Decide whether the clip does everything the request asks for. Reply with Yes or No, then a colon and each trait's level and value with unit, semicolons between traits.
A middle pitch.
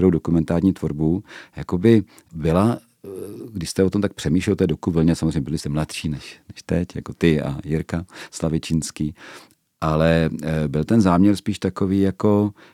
No: very low, 85 Hz